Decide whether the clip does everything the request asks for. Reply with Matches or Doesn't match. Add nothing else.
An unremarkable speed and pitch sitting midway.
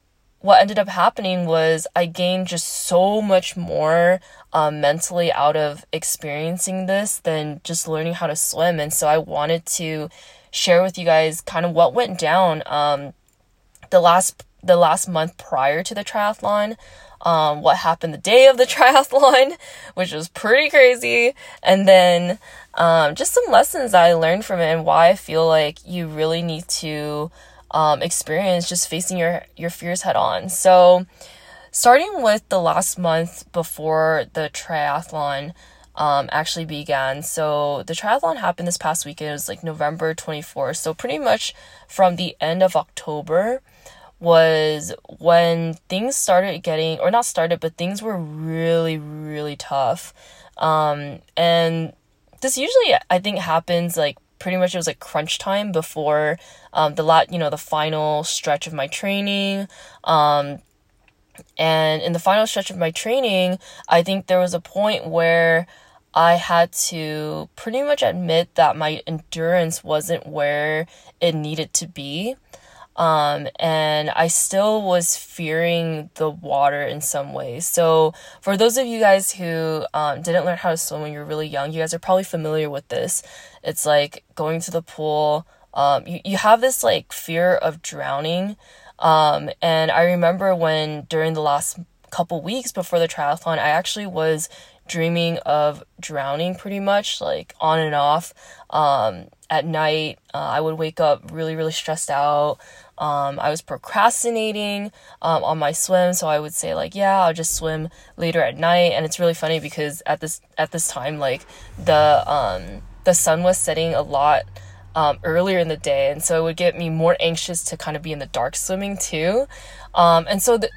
Matches